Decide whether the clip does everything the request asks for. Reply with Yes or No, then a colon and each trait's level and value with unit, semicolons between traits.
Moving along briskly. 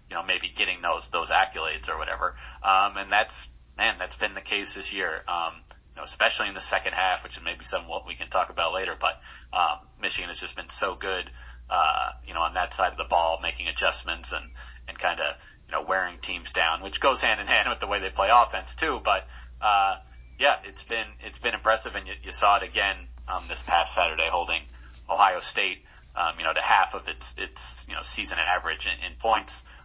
Yes: fast, 225 wpm